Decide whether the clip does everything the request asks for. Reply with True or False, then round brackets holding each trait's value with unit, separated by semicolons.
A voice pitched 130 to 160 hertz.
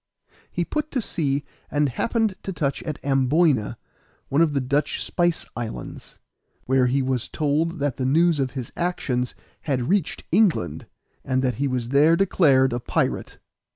True (140 Hz)